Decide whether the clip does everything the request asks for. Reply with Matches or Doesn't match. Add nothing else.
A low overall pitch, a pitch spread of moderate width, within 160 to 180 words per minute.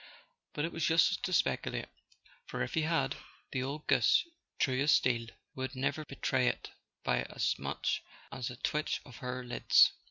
Matches